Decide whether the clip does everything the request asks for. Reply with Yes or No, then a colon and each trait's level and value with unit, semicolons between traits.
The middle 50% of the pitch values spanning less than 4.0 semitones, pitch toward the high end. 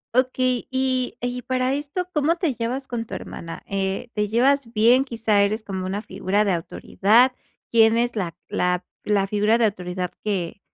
No: average, 4.3 semitones; high, 225 Hz